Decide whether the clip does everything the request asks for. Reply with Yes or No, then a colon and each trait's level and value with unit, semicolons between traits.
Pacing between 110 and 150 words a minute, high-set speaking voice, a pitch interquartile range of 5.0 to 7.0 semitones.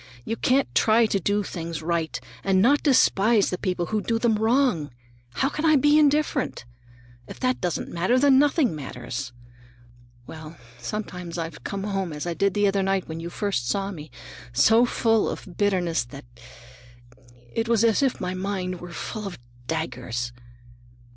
No: average, 165 wpm; high, 195 Hz; wide, 5.4 semitones